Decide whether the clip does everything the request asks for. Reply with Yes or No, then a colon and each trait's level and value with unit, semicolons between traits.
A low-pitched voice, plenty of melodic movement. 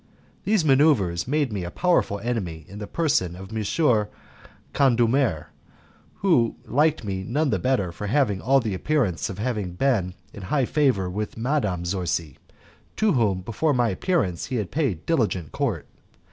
Yes: low, 110 Hz; wide, 6.9 semitones